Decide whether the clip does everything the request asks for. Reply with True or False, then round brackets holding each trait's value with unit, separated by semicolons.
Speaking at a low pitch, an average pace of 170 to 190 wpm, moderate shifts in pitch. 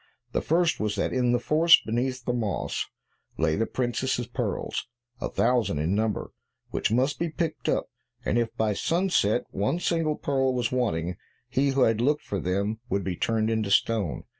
True (120 Hz; 180 wpm; 4.1 semitones)